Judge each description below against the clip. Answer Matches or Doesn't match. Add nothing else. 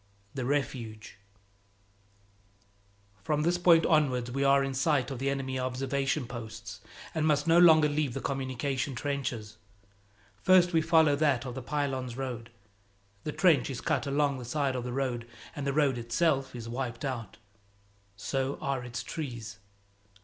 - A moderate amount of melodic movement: Matches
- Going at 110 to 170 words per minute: Matches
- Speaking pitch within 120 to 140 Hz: Matches